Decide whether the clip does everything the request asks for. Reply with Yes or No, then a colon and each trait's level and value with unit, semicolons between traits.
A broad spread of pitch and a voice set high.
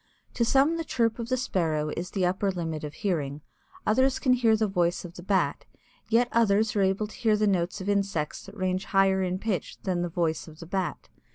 No: average, 3.9 semitones; high, 195 Hz